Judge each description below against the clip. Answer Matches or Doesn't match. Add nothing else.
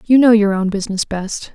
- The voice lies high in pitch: Matches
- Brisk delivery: Matches